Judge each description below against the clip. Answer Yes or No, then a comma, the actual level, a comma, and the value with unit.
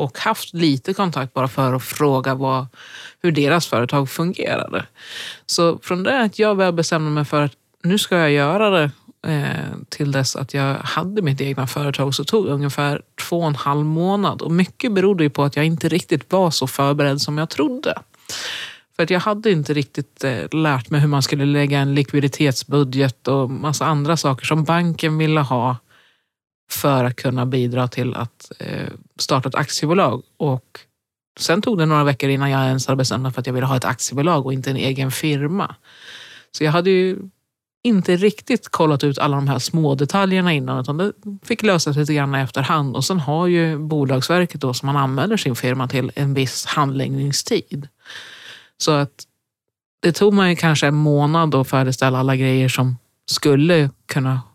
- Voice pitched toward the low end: No, medium, 145 Hz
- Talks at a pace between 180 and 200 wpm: Yes, average, 185 wpm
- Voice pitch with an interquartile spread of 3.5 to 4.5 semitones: Yes, average, 3.9 semitones